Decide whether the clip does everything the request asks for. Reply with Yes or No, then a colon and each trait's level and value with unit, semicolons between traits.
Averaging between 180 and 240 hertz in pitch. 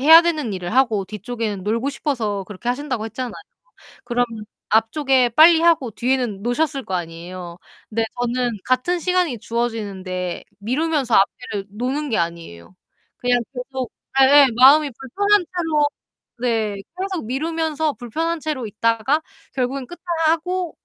No: very high, 250 Hz